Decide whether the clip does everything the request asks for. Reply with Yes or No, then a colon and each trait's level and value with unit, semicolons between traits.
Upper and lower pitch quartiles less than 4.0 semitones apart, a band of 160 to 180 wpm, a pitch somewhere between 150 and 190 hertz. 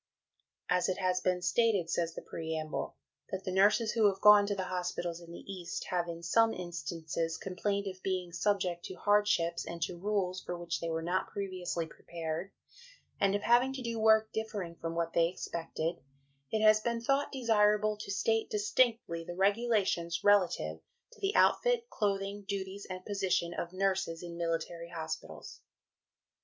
Yes: average, 3.6 semitones; average, 170 wpm; medium, 185 Hz